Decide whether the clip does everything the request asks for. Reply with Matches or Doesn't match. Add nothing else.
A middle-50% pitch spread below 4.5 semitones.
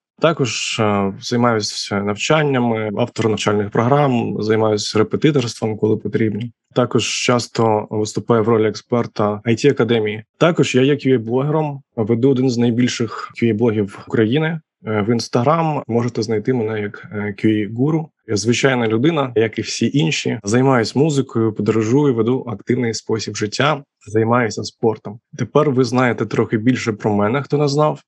Matches